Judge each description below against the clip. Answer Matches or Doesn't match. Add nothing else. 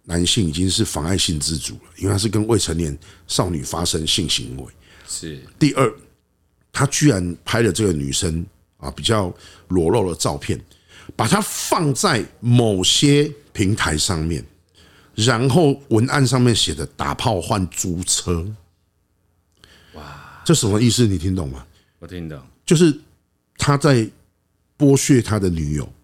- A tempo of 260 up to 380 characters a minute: Doesn't match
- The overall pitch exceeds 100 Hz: Doesn't match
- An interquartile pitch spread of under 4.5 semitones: Doesn't match